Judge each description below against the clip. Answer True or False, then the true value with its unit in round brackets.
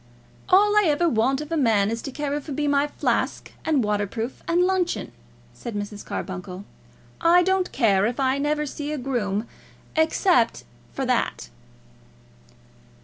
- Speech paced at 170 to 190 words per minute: False (150 wpm)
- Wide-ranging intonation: True (6.4 semitones)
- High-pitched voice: True (275 Hz)